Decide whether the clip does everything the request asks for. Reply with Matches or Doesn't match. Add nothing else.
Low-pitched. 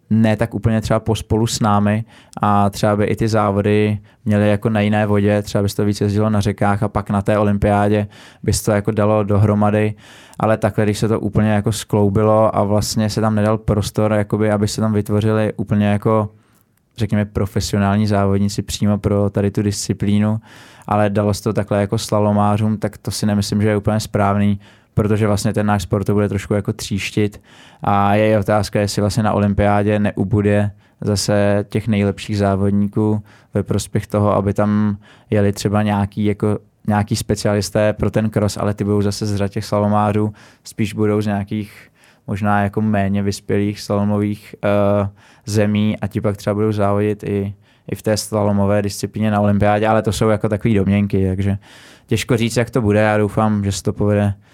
Matches